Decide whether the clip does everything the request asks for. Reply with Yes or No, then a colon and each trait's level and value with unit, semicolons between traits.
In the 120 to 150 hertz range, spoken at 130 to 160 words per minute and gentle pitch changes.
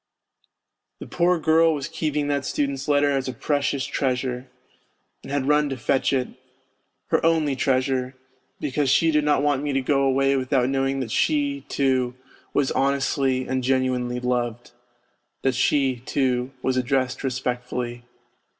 Yes: low, 135 Hz; average, 150 wpm; narrow, 2.0 semitones